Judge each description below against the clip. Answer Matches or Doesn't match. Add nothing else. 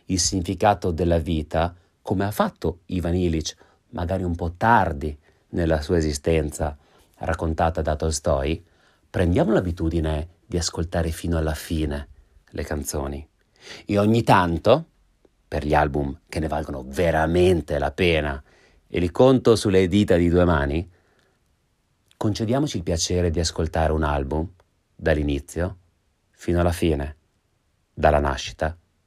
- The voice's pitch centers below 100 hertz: Matches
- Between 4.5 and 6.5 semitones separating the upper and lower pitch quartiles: Doesn't match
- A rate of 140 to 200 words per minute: Doesn't match